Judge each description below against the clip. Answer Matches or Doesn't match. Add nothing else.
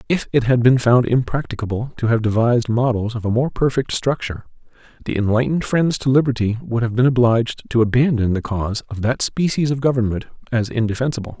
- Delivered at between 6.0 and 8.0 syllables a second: Matches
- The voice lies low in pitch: Matches